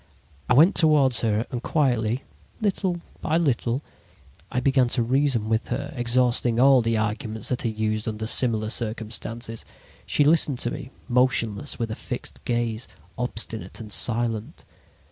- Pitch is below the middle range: Yes, low, 120 Hz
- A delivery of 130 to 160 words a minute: Yes, average, 145 wpm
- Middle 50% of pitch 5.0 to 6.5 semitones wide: No, average, 3.0 semitones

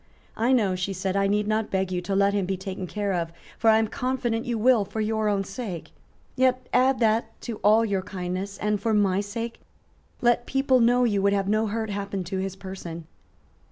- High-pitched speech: Yes, high, 205 Hz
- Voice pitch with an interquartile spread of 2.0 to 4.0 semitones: Yes, average, 2.9 semitones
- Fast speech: Yes, fast, 215 wpm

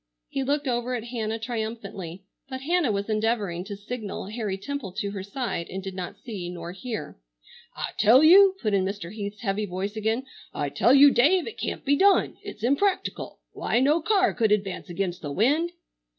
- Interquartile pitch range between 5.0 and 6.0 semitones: Yes, wide, 5.4 semitones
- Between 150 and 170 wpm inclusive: No, average, 190 wpm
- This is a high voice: Yes, high, 220 Hz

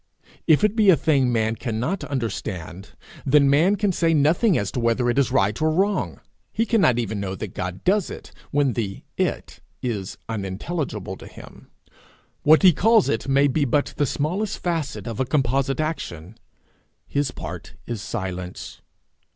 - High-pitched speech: No, low, 135 Hz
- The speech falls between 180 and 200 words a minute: No, average, 165 wpm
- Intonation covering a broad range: Yes, wide, 6.6 semitones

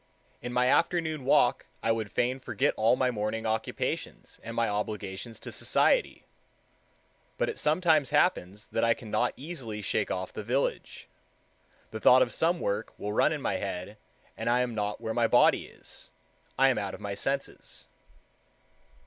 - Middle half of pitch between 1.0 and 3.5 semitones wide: No, average, 4.0 semitones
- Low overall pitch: Yes, low, 115 Hz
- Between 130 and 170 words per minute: Yes, average, 165 wpm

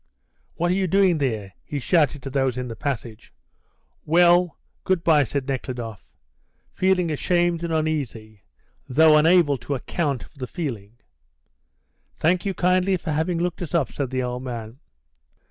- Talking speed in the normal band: Yes, average, 155 wpm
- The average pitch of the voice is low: No, medium, 150 Hz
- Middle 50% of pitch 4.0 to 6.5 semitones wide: Yes, wide, 5.5 semitones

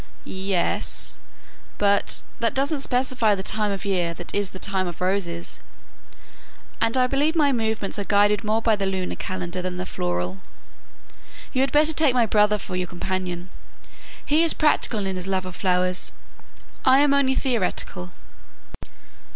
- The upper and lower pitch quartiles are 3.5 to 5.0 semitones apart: No, wide, 5.5 semitones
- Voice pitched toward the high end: Yes, high, 200 Hz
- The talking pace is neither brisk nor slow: Yes, average, 160 wpm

